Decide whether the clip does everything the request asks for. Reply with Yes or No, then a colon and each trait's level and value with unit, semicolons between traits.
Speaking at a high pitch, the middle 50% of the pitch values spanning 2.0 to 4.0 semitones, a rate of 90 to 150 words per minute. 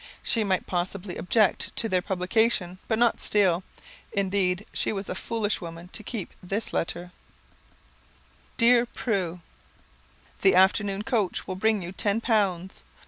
Yes: high, 195 Hz; average, 3.3 semitones; average, 140 wpm